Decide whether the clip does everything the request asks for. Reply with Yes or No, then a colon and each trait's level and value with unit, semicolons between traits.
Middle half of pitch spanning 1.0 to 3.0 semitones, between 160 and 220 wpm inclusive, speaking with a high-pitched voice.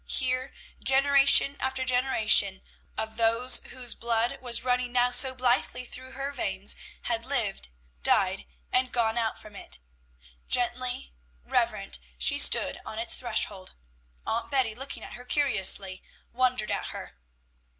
No: average, 2.7 semitones; slow, 135 wpm; high, 245 Hz